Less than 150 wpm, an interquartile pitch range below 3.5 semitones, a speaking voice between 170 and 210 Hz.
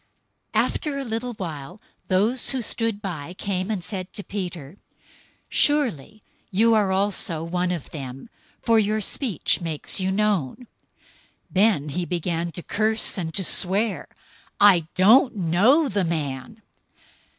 No: average, 140 wpm; average, 4.3 semitones; high, 190 Hz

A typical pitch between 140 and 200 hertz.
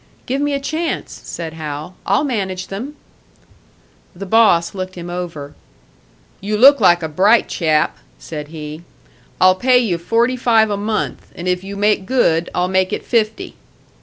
Yes: high, 190 Hz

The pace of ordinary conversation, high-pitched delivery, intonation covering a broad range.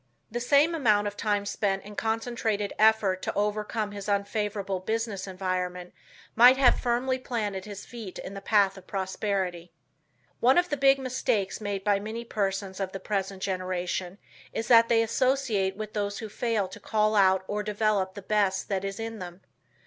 No: average, 175 wpm; high, 205 Hz; average, 2.7 semitones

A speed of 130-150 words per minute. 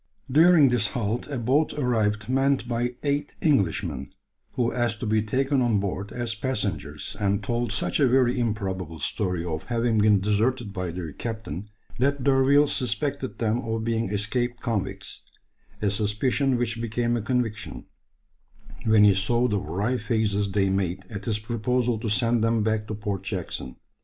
No: average, 160 wpm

